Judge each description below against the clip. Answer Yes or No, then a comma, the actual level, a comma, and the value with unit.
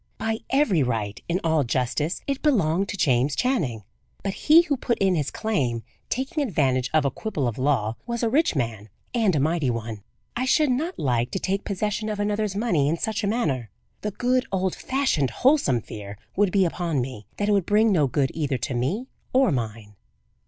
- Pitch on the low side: No, medium, 175 Hz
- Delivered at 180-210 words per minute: Yes, average, 200 wpm